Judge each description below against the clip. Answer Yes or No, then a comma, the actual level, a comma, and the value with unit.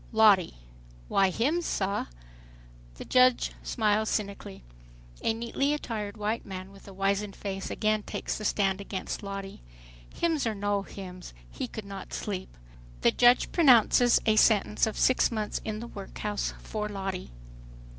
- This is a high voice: Yes, high, 210 Hz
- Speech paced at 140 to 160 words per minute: Yes, average, 145 wpm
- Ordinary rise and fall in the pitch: No, narrow, 2.3 semitones